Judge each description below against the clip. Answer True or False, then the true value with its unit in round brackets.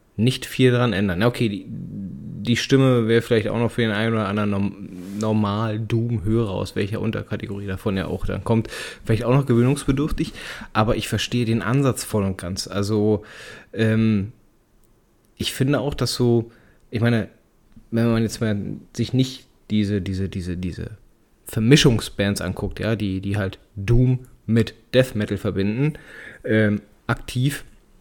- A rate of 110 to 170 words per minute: True (155 wpm)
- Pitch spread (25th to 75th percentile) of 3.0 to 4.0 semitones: False (2.6 semitones)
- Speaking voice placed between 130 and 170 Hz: False (110 Hz)